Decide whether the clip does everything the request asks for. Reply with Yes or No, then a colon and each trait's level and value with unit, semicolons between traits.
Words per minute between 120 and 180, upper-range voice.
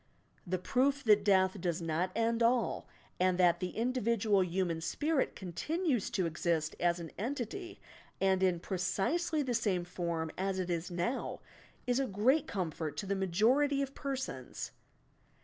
Yes: average, 150 wpm; high, 195 Hz